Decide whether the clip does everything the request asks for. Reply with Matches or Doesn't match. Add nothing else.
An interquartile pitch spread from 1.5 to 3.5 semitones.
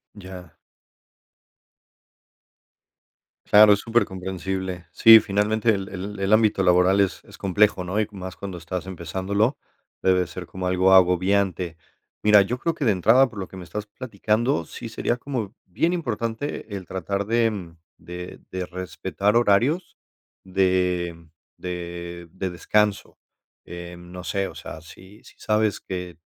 Matches